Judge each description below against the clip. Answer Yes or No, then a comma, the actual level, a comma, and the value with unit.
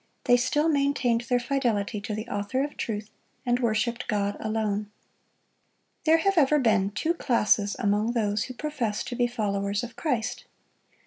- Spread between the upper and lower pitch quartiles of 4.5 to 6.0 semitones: No, average, 3.7 semitones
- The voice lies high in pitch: Yes, high, 235 Hz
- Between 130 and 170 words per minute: Yes, average, 155 wpm